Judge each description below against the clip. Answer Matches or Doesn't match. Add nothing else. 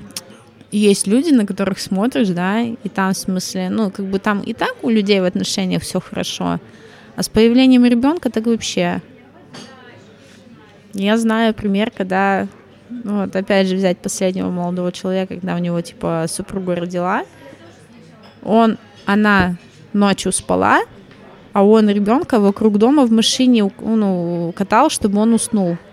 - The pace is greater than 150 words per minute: Doesn't match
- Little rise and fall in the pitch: Doesn't match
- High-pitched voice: Matches